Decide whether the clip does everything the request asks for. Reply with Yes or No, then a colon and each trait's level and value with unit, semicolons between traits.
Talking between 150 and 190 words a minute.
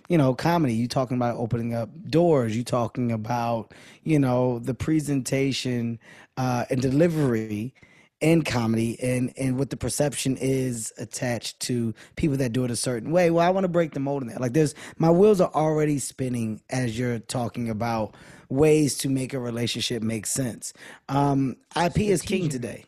Yes: average, 180 wpm